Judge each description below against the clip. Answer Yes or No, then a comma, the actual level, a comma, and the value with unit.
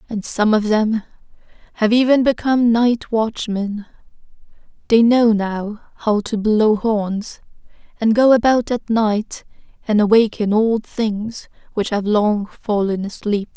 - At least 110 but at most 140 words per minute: Yes, slow, 135 wpm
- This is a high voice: Yes, high, 220 Hz